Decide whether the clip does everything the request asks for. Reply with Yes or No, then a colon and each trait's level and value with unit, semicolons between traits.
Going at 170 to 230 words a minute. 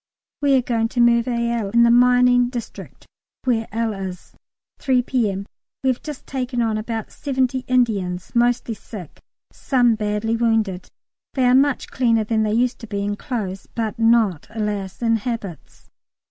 No: average, 160 wpm